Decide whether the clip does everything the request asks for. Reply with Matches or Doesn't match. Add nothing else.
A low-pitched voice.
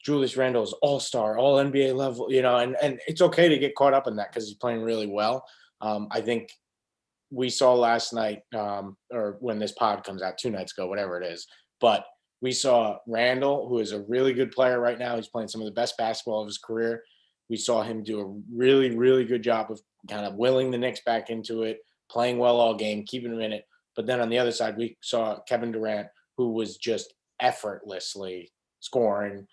Matches